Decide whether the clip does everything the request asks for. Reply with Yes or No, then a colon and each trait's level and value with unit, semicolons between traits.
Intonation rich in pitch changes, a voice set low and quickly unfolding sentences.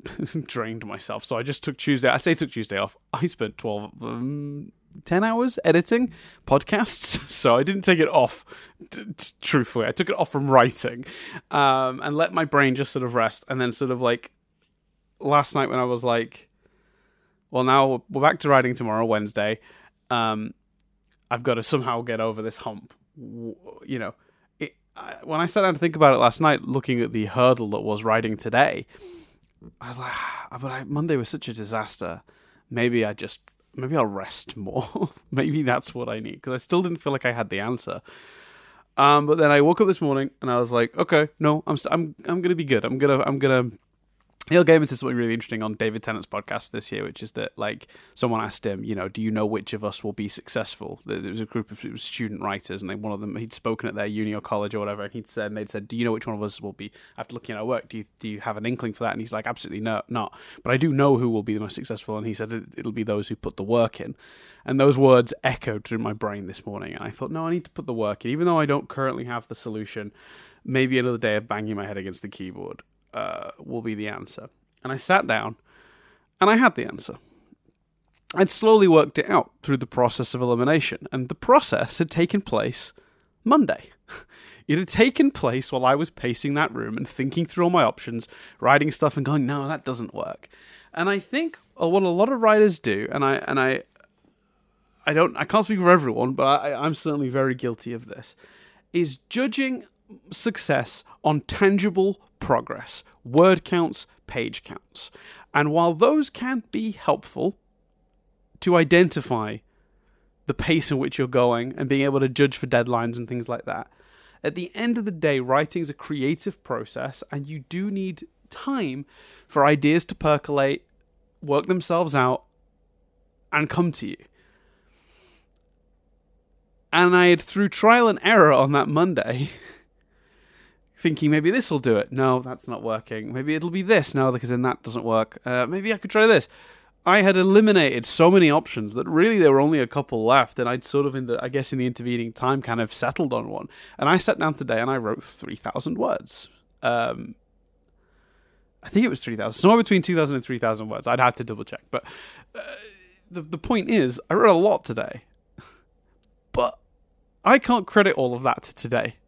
Yes: wide, 6.4 semitones; low, 130 Hz; fast, 210 wpm